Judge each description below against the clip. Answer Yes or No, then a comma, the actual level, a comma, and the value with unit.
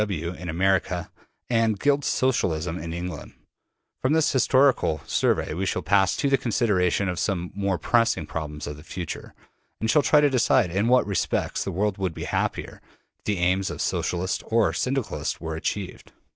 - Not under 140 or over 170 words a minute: No, average, 185 wpm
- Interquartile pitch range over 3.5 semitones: Yes, average, 5.0 semitones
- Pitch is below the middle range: Yes, very low, 95 Hz